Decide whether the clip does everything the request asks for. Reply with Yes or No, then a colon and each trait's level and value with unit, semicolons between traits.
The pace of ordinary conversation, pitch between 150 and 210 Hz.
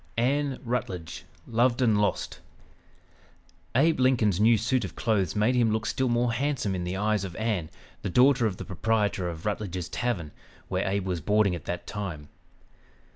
No: average, 170 wpm; low, 105 Hz